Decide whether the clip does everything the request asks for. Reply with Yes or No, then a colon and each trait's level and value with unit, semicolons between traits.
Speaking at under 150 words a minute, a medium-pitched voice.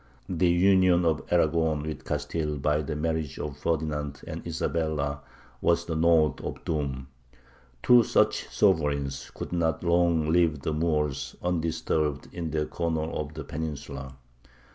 No: average, 140 wpm; very low, 80 Hz